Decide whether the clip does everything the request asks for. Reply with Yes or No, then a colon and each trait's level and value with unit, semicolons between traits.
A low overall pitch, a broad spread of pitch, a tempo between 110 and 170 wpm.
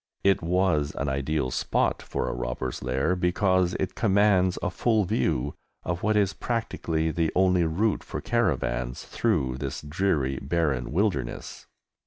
Yes: very low, 85 Hz; wide, 6.1 semitones; average, 145 wpm